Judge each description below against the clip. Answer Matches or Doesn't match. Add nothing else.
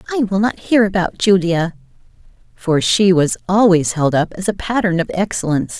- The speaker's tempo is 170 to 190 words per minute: Matches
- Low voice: Doesn't match